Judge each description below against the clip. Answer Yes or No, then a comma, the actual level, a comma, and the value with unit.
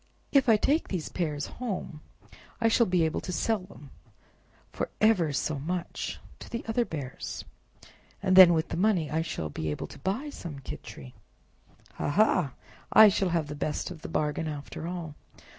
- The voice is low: No, medium, 170 Hz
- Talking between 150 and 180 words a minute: Yes, average, 175 wpm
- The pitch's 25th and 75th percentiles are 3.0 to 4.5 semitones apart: No, wide, 5.4 semitones